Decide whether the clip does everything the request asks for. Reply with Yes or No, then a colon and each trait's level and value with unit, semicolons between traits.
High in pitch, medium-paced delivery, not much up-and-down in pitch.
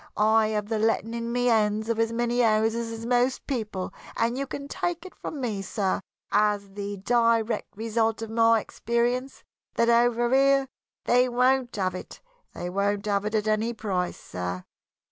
Yes: high, 225 Hz; average, 170 wpm; narrow, 2.3 semitones